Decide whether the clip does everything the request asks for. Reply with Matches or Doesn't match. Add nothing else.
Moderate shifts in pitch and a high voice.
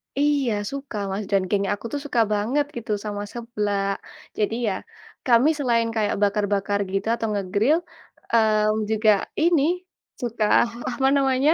Matches